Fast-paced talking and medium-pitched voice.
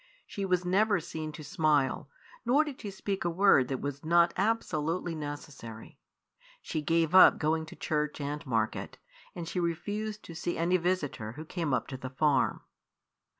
No: average, 170 wpm; medium, 165 Hz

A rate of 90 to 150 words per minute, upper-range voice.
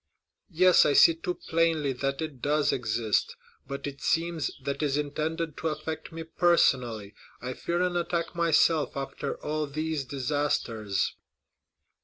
No: average, 145 wpm; medium, 150 Hz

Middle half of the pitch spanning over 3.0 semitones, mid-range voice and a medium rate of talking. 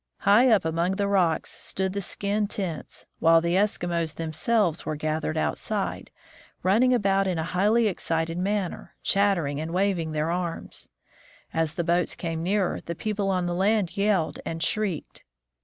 Yes: average, 3.5 semitones; medium, 180 Hz; average, 155 wpm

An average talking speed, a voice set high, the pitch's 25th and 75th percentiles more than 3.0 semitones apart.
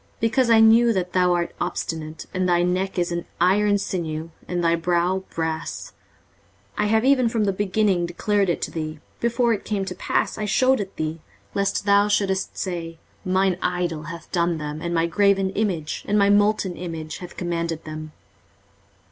No: average, 185 wpm; medium, 180 Hz; average, 3.4 semitones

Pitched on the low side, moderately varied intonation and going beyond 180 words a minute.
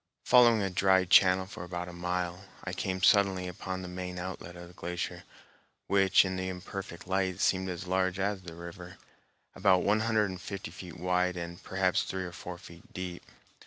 No: very low, 90 Hz; narrow, 1.3 semitones; average, 190 wpm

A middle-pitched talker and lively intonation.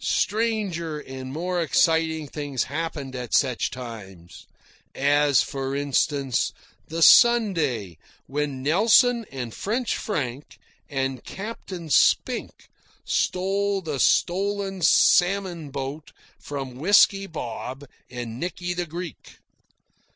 Yes: medium, 150 Hz; wide, 5.7 semitones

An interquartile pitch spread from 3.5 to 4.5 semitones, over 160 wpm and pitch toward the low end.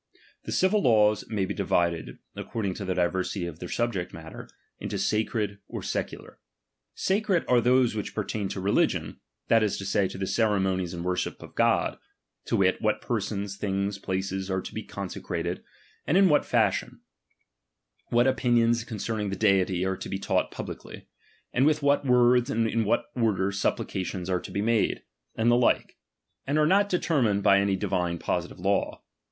Yes: average, 3.9 semitones; average, 175 wpm; low, 105 Hz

